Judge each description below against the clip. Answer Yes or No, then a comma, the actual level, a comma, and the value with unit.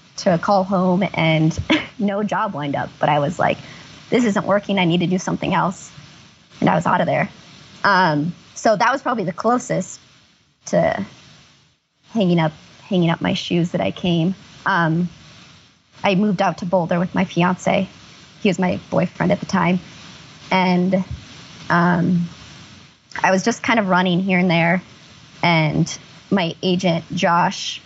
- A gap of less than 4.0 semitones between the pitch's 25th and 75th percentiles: Yes, narrow, 2.4 semitones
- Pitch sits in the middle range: Yes, medium, 180 Hz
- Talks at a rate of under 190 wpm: Yes, average, 160 wpm